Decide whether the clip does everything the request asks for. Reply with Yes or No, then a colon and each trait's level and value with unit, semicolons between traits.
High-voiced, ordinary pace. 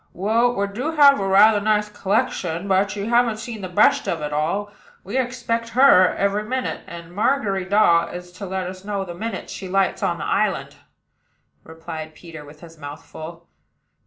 Yes: high, 195 Hz; average, 180 wpm